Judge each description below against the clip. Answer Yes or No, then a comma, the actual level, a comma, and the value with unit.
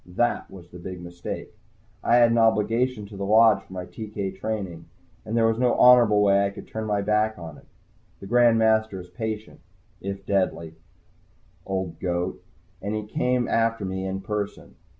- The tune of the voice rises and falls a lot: No, average, 2.9 semitones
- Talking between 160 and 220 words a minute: Yes, average, 185 wpm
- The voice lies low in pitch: Yes, low, 105 Hz